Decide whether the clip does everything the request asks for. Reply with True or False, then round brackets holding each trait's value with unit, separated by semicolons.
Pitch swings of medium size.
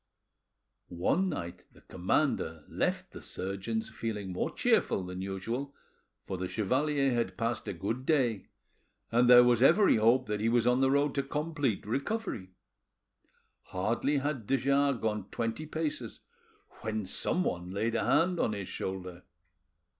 False (6.1 semitones)